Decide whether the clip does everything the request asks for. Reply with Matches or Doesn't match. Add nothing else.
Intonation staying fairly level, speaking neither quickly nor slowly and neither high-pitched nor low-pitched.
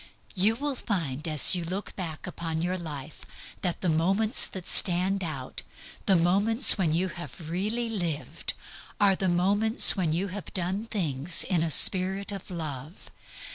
Doesn't match